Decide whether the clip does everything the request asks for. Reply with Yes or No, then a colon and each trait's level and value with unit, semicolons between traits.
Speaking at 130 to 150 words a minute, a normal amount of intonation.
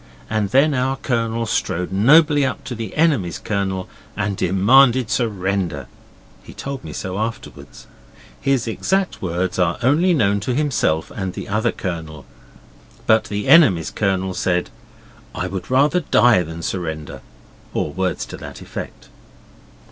No: average, 140 wpm; wide, 6.1 semitones